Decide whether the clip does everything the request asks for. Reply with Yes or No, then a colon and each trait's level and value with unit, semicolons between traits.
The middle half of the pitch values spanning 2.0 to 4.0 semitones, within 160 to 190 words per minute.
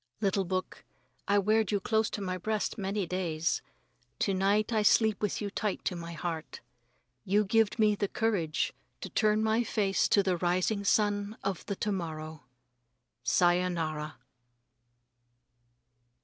No: average, 3.0 semitones; average, 145 wpm